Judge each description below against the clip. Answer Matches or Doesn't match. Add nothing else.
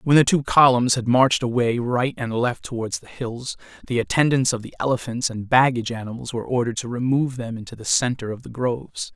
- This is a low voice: Matches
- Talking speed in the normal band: Doesn't match